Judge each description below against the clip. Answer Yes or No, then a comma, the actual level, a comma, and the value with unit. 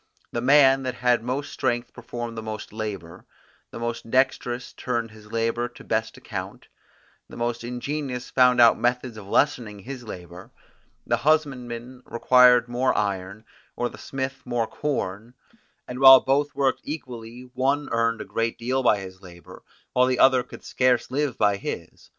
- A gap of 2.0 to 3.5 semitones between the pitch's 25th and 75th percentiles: Yes, narrow, 2.4 semitones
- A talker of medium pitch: No, low, 120 Hz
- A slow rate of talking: No, average, 160 wpm